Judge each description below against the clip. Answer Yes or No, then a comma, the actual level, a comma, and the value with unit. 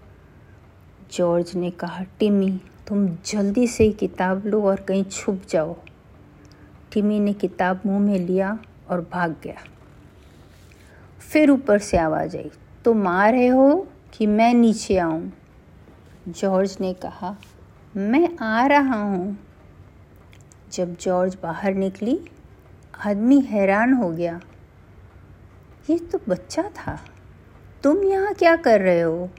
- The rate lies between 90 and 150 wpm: Yes, average, 125 wpm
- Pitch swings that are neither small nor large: Yes, average, 4.3 semitones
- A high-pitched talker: Yes, high, 195 Hz